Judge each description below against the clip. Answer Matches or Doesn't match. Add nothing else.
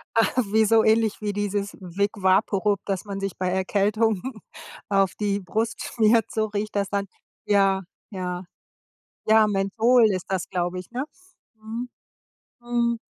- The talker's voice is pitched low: Doesn't match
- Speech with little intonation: Matches